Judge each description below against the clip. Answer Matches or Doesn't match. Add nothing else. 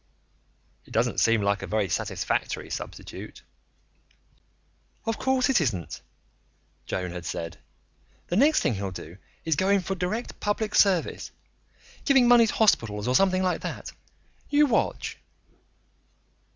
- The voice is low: Doesn't match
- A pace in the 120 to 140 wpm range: Matches